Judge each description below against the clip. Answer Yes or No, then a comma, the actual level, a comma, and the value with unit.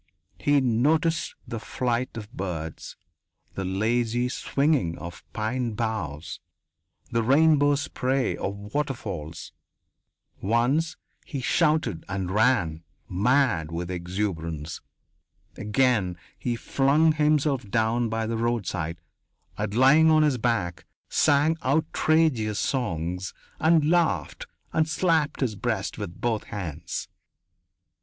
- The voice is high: No, low, 115 Hz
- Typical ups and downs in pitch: No, wide, 7.0 semitones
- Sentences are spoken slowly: Yes, slow, 105 wpm